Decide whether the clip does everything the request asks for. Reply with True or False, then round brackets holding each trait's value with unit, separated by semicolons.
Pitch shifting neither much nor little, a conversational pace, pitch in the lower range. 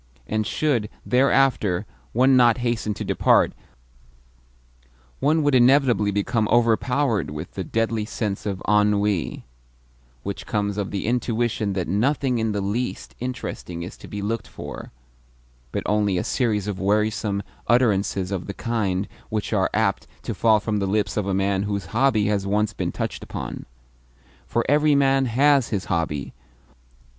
True (3.4 semitones; 150 wpm; 105 Hz)